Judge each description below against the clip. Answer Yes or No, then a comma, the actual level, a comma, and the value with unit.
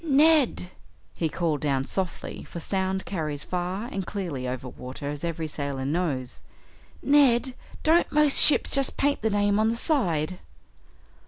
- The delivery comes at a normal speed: Yes, average, 150 wpm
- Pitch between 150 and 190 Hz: Yes, medium, 185 Hz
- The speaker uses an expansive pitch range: Yes, wide, 8.1 semitones